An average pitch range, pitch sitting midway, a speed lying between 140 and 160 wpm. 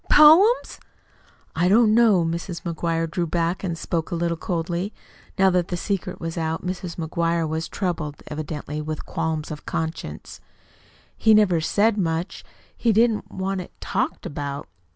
Yes: average, 3.0 semitones; medium, 170 Hz; average, 150 wpm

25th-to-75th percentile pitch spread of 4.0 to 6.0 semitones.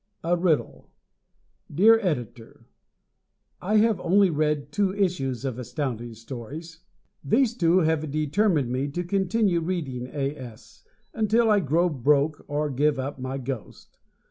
Yes: wide, 5.6 semitones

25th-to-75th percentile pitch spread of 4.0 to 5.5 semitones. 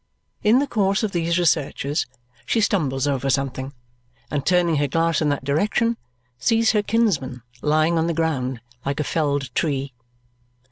Yes: average, 5.1 semitones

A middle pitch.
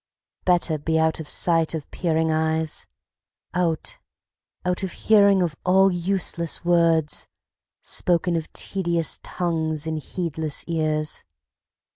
Yes: medium, 165 Hz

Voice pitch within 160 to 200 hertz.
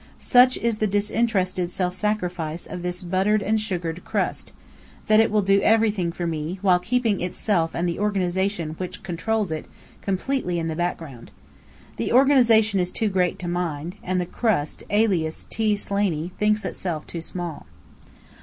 Yes: medium, 185 Hz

